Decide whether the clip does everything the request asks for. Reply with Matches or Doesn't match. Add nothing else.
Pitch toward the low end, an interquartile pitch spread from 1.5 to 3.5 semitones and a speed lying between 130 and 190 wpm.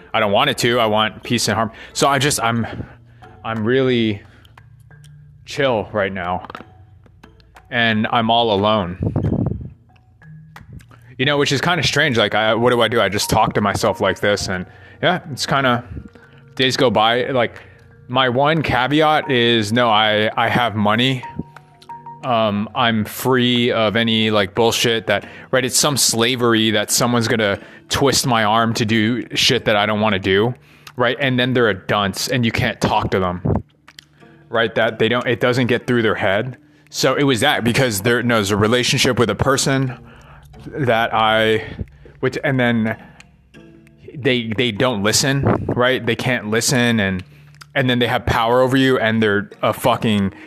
Matches